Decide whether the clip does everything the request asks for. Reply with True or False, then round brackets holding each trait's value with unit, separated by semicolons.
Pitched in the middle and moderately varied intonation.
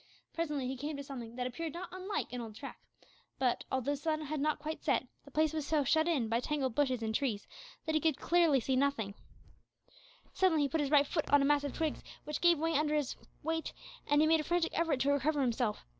False (290 Hz; 3.1 semitones)